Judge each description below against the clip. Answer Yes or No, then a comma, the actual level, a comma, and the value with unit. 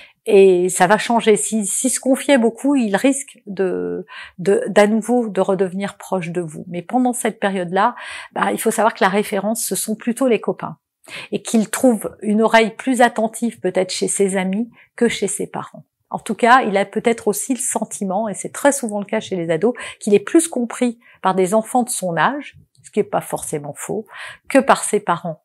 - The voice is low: No, high, 215 Hz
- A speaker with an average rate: Yes, average, 210 wpm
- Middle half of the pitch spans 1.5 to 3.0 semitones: No, average, 3.6 semitones